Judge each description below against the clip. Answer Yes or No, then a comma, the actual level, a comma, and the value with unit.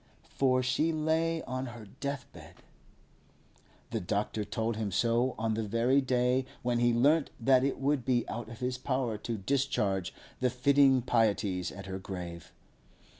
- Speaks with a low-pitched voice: Yes, low, 120 Hz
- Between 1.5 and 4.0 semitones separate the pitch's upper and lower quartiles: Yes, average, 3.5 semitones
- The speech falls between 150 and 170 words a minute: Yes, average, 155 wpm